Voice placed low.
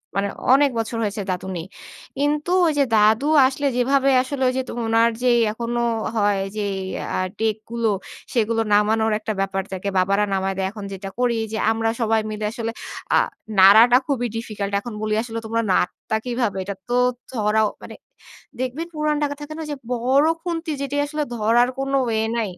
No: high, 225 Hz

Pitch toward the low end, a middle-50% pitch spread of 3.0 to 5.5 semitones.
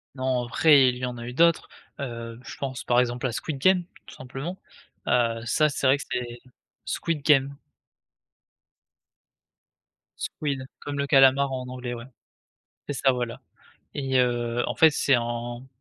No: low, 130 Hz; narrow, 2.5 semitones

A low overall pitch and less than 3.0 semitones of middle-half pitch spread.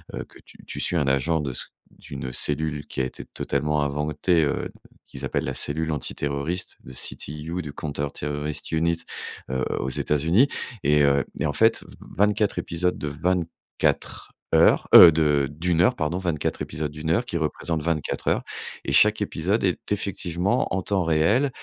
No: very low, 80 Hz; average, 3.5 semitones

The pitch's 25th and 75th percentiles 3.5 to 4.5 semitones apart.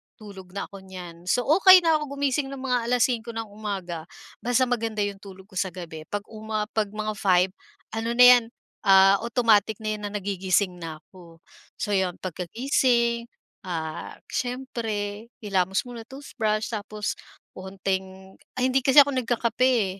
Yes: average, 4.1 semitones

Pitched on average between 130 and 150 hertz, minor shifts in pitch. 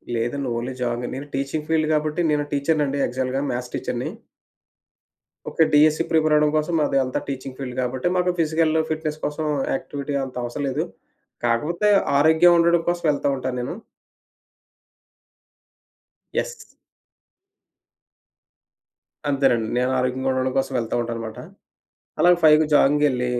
No: medium, 140 Hz; average, 3.5 semitones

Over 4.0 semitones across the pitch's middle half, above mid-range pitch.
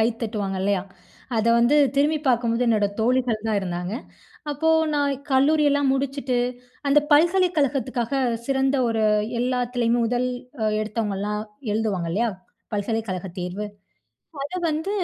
Yes: average, 4.6 semitones; high, 240 Hz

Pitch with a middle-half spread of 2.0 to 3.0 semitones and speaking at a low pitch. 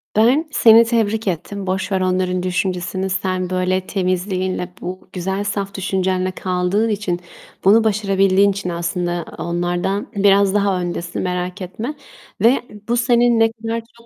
No: narrow, 2.5 semitones; high, 190 Hz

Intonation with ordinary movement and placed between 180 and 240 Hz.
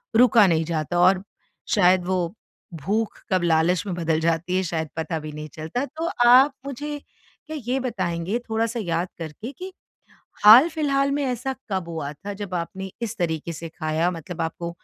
No: wide, 6.3 semitones; medium, 185 Hz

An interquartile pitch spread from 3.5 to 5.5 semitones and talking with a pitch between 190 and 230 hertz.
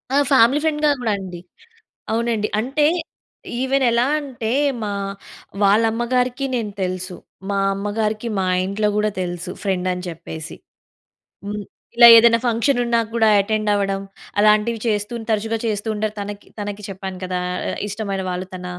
No: average, 3.1 semitones; high, 210 Hz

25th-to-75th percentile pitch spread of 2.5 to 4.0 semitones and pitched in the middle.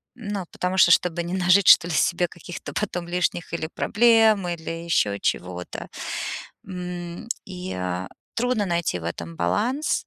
Yes: average, 3.0 semitones; medium, 175 Hz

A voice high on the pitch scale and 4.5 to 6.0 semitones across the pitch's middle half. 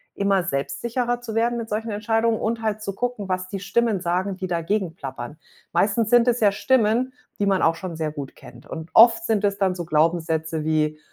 Yes: high, 200 Hz; average, 5.3 semitones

